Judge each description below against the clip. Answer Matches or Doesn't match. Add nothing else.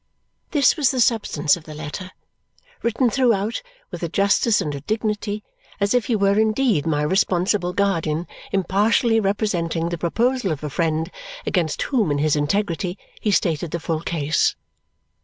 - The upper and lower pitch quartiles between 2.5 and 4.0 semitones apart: Doesn't match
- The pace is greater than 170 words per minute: Doesn't match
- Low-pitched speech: Doesn't match